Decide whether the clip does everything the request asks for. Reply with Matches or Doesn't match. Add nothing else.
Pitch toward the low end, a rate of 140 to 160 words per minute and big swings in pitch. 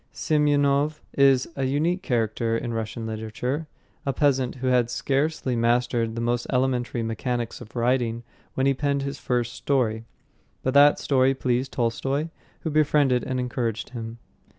Doesn't match